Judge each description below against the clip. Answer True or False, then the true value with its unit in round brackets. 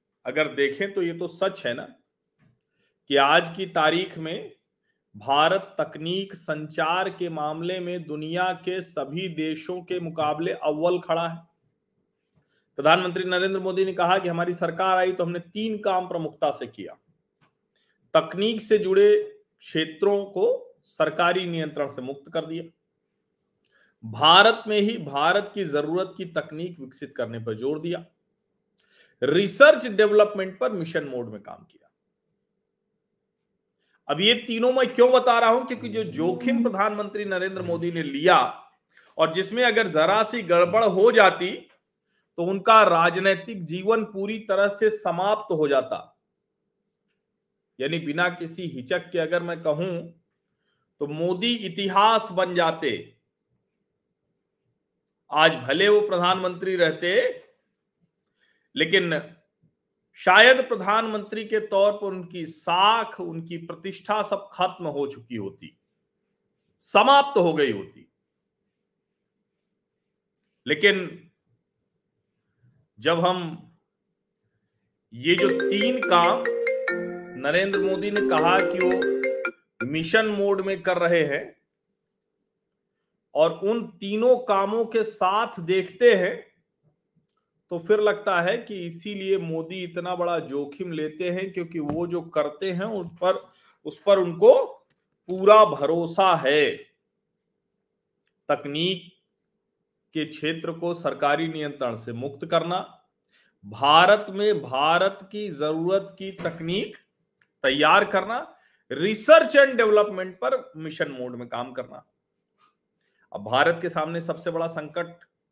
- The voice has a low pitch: False (185 Hz)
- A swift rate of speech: False (125 wpm)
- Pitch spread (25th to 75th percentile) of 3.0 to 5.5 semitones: True (4.1 semitones)